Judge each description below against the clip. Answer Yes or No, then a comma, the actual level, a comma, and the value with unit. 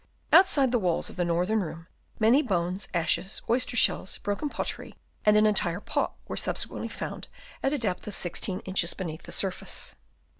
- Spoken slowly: No, average, 175 wpm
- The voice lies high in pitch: Yes, high, 195 Hz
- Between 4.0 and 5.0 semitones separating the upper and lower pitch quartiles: Yes, average, 4.4 semitones